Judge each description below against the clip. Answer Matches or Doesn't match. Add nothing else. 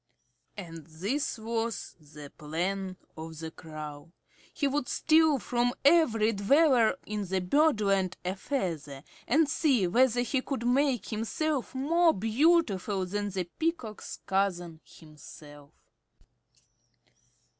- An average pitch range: Doesn't match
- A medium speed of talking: Doesn't match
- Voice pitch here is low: Doesn't match